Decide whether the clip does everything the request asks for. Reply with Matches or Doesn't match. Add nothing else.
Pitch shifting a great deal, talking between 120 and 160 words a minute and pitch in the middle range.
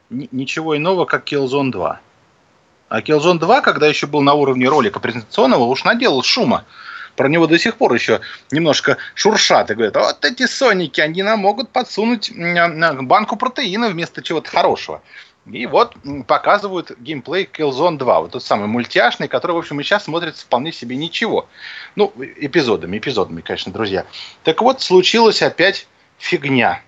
Matches